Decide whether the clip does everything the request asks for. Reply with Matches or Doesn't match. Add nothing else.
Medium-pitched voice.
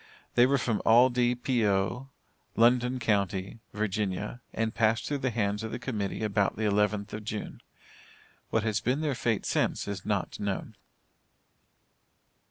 Doesn't match